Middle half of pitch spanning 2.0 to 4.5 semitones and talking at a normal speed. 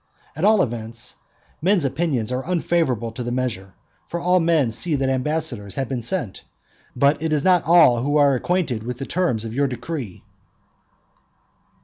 No: wide, 5.6 semitones; average, 165 wpm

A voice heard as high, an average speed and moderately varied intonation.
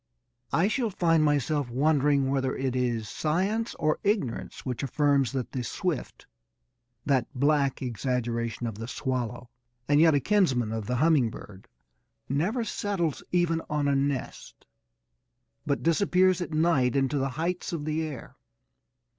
No: medium, 145 Hz; average, 145 wpm; average, 4.6 semitones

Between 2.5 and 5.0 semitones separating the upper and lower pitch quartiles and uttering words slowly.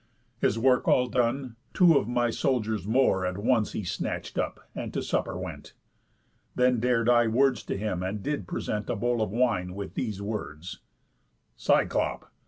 No: average, 3.7 semitones; average, 170 wpm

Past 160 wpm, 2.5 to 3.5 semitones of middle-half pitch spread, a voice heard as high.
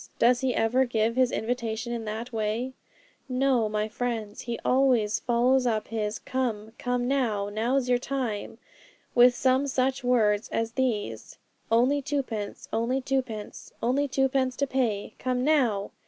No: average, 145 wpm; average, 2.9 semitones; high, 245 Hz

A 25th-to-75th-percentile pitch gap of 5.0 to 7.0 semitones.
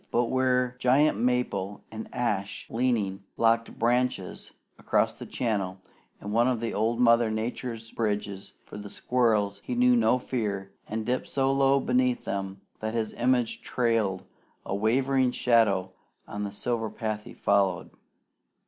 No: average, 3.4 semitones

